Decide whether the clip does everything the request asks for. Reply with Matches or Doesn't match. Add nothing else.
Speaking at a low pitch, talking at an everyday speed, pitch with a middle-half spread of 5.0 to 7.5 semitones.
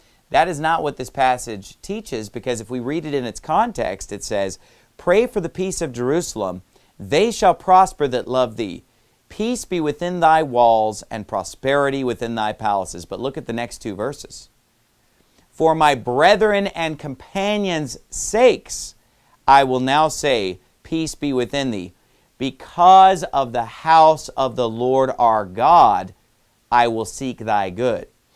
Matches